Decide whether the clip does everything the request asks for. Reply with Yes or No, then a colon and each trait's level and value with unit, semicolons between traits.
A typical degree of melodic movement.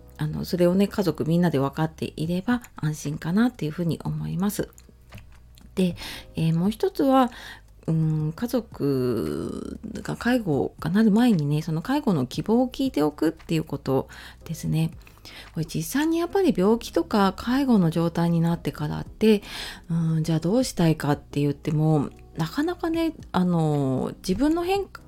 No: wide, 7.1 semitones